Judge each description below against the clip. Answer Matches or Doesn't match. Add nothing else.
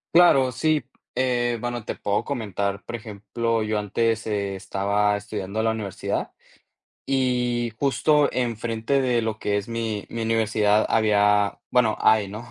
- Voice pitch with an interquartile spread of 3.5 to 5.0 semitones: Doesn't match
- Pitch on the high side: Doesn't match